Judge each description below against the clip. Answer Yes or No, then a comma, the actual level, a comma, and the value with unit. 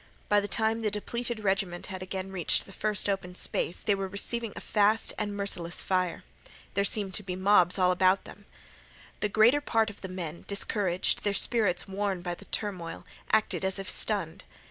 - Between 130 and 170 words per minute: No, average, 190 wpm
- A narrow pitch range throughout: Yes, narrow, 2.2 semitones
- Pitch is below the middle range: No, high, 200 Hz